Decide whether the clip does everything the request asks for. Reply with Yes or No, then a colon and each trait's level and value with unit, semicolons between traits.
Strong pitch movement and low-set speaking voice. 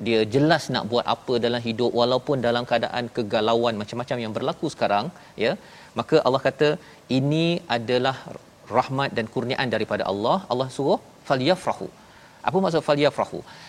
No: average, 3.3 semitones; low, 125 Hz